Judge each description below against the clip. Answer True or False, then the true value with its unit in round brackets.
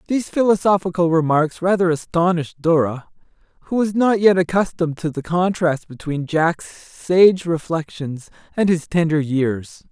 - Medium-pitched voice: True (170 Hz)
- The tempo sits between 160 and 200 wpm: False (135 wpm)